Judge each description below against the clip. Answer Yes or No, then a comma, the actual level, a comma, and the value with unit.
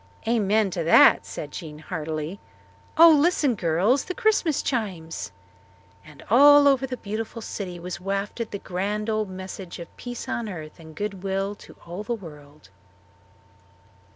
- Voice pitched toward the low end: No, high, 200 Hz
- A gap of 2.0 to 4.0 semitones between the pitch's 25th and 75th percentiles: No, wide, 5.5 semitones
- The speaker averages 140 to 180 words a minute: Yes, average, 150 wpm